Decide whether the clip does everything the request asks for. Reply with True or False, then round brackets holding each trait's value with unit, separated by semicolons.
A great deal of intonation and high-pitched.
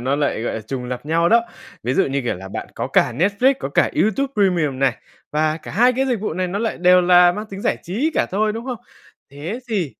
False (7.4 semitones; 180 Hz)